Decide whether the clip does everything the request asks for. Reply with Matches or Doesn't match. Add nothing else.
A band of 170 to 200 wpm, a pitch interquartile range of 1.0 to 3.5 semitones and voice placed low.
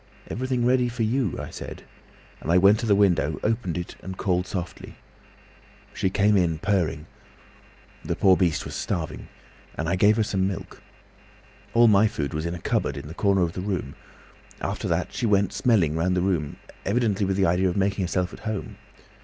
Matches